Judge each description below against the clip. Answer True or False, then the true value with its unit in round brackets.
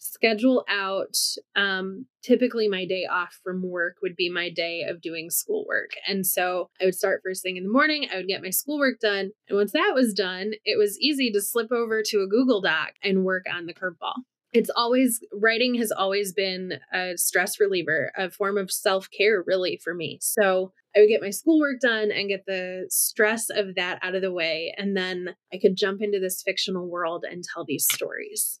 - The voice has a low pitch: False (195 Hz)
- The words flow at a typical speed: False (210 wpm)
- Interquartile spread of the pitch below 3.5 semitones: False (3.8 semitones)